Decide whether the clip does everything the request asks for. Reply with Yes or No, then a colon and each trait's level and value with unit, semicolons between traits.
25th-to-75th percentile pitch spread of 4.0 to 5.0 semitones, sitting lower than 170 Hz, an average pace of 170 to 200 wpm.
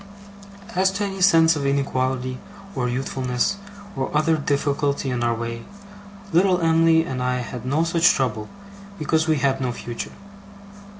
No: average, 4.4 semitones; medium, 140 Hz; average, 145 wpm